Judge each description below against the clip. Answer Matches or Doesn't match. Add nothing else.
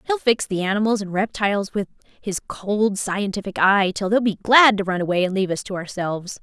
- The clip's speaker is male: Doesn't match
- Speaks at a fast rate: Matches